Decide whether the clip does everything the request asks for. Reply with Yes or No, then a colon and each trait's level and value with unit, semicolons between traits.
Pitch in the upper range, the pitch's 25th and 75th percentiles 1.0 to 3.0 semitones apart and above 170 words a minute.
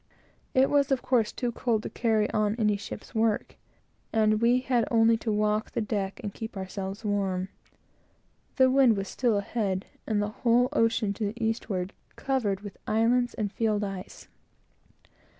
No: high, 220 Hz; narrow, 2.5 semitones; average, 165 wpm